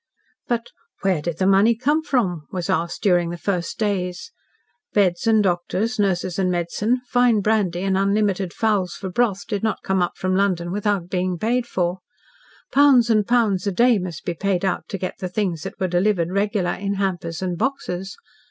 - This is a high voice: Yes, high, 195 Hz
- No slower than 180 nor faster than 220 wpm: Yes, average, 185 wpm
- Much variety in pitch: No, average, 3.3 semitones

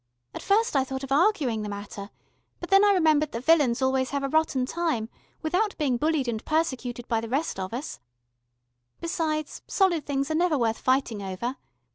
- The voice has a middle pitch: No, very high, 275 Hz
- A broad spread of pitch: No, average, 5.0 semitones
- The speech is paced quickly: No, average, 185 wpm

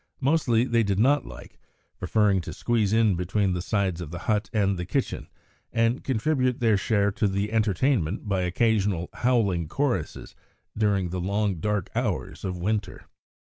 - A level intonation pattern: No, average, 3.6 semitones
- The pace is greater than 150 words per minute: Yes, average, 160 wpm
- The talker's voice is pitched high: No, low, 105 Hz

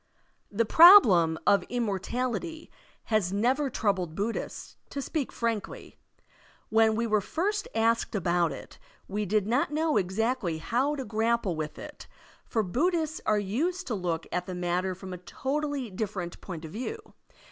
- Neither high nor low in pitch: No, high, 220 Hz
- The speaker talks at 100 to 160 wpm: Yes, average, 150 wpm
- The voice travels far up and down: Yes, wide, 6.1 semitones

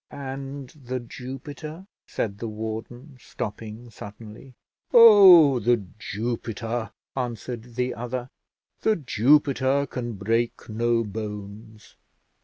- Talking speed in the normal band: No, slow, 95 wpm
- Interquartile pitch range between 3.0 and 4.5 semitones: Yes, average, 3.4 semitones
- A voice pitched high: No, low, 120 Hz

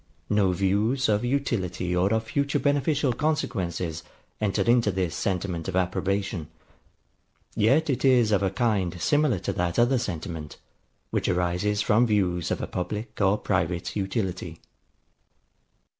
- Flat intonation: No, average, 4.8 semitones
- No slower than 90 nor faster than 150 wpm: Yes, slow, 135 wpm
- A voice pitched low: Yes, low, 100 Hz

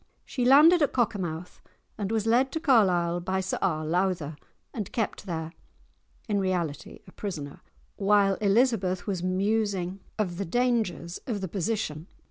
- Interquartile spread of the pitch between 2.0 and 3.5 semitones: No, average, 4.2 semitones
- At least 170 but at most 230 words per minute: No, average, 145 wpm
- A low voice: No, high, 195 Hz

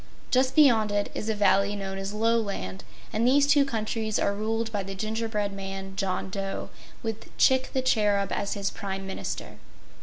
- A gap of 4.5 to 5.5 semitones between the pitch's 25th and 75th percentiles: No, narrow, 2.5 semitones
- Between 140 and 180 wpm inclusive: Yes, average, 175 wpm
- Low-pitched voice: No, high, 210 Hz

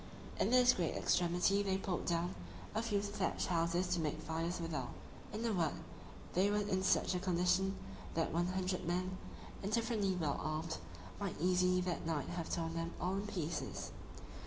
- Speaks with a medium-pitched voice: Yes, medium, 180 Hz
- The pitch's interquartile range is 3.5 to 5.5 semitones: No, narrow, 2.5 semitones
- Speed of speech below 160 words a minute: No, average, 170 wpm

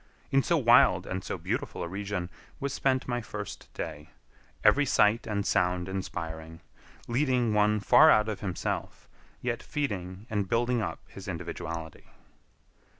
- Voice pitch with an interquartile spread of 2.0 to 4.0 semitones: No, average, 5.1 semitones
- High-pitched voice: No, low, 105 Hz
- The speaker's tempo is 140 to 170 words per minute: Yes, average, 145 wpm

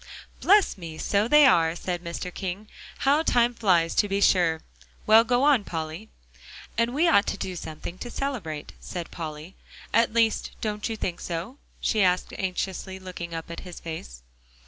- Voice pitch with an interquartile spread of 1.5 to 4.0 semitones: No, average, 5.3 semitones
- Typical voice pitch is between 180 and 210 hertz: Yes, high, 190 Hz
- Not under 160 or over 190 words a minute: Yes, average, 170 wpm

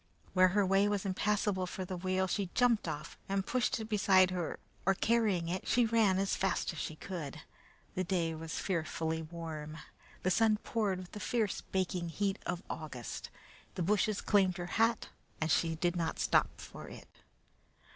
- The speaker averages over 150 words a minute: Yes, average, 175 wpm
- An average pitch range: Yes, average, 3.3 semitones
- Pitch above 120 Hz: Yes, medium, 185 Hz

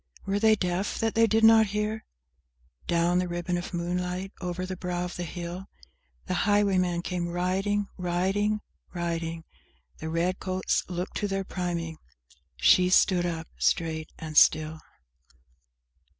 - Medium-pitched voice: Yes, medium, 180 Hz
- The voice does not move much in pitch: Yes, narrow, 2.2 semitones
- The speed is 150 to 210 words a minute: No, average, 140 wpm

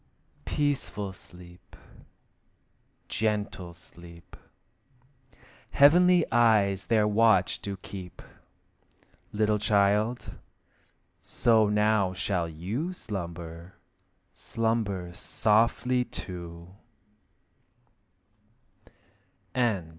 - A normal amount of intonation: Yes, average, 4.0 semitones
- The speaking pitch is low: Yes, low, 105 Hz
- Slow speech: Yes, slow, 60 wpm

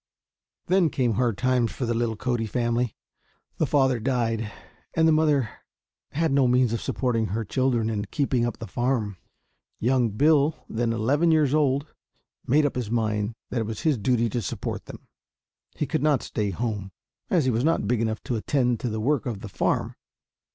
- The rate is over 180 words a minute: Yes, average, 190 wpm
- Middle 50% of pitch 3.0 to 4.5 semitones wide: Yes, average, 3.4 semitones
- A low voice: Yes, low, 120 Hz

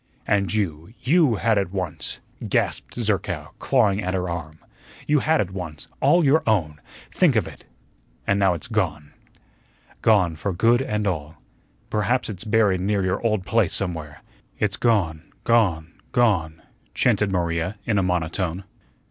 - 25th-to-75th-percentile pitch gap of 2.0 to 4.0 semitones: No, average, 4.5 semitones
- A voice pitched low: Yes, very low, 95 Hz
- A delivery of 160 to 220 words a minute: No, average, 150 wpm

